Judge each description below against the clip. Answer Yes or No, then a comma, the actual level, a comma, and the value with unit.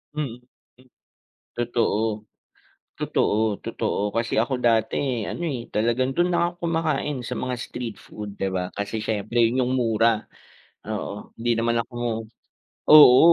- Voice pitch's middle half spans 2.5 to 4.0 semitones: Yes, average, 2.8 semitones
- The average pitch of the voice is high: No, low, 115 Hz